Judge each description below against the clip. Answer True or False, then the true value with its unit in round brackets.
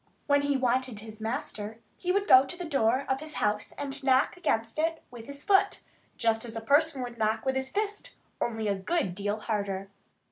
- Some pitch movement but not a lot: True (4.6 semitones)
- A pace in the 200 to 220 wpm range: True (205 wpm)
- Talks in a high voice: True (255 Hz)